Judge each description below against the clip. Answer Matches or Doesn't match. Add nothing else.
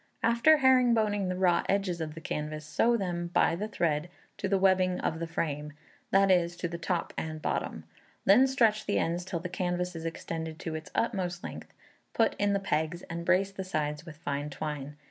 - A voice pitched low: Doesn't match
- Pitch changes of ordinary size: Matches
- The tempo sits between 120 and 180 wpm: Doesn't match